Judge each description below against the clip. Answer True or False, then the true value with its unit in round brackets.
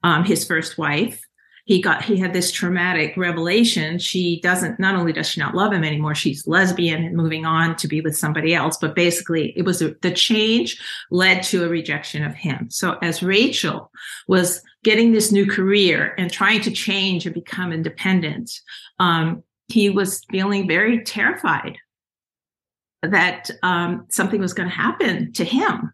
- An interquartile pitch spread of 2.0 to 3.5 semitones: True (2.8 semitones)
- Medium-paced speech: True (170 wpm)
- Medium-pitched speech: True (180 Hz)